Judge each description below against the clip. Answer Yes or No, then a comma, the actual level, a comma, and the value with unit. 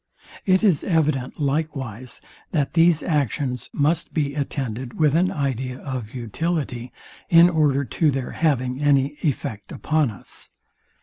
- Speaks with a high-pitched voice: No, medium, 140 Hz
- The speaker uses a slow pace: Yes, slow, 130 wpm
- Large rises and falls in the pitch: No, average, 3.6 semitones